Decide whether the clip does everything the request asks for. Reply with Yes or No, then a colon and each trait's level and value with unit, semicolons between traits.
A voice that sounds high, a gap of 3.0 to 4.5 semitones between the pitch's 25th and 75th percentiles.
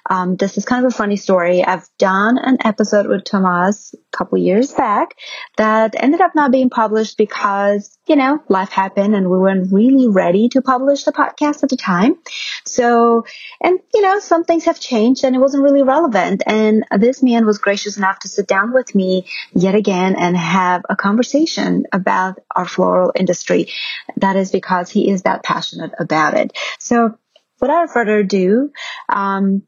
No: high, 215 Hz; wide, 5.4 semitones